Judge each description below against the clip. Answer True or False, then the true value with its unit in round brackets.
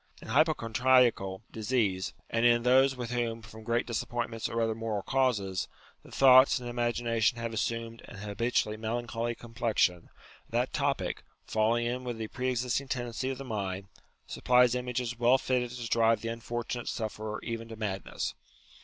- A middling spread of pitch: False (1.9 semitones)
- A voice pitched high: False (115 Hz)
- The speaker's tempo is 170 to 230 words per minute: False (155 wpm)